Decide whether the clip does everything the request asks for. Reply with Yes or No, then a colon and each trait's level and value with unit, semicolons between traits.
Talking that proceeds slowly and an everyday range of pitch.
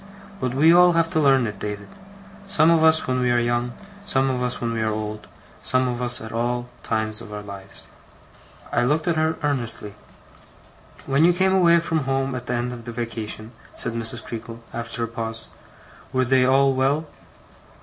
No: average, 195 wpm; average, 3.5 semitones